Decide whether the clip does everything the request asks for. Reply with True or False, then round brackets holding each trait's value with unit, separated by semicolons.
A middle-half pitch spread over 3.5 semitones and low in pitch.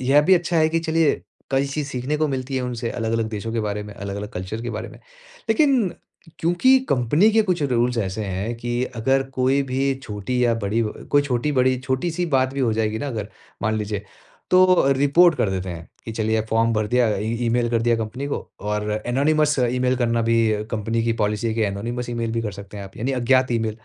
True (4.0 semitones; 120 Hz)